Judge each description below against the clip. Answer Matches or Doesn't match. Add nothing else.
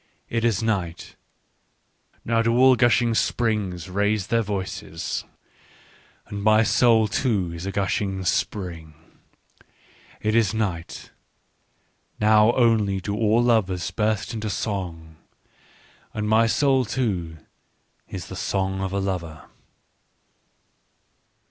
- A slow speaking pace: Matches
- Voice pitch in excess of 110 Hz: Doesn't match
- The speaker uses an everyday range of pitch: Matches